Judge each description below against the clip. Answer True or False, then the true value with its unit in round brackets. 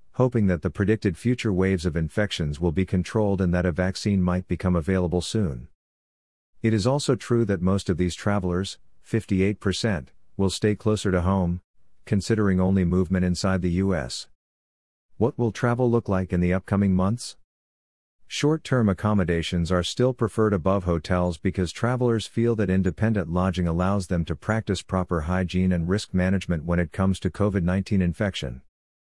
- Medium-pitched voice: False (95 Hz)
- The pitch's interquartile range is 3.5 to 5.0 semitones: False (3.0 semitones)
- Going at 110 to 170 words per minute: True (165 wpm)